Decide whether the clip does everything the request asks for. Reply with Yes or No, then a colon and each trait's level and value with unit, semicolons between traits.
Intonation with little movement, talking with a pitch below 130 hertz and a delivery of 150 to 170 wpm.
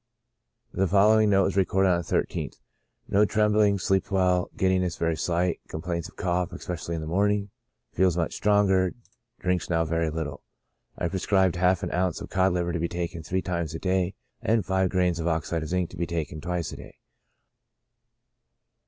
No: narrow, 2.1 semitones; very low, 90 Hz; average, 190 wpm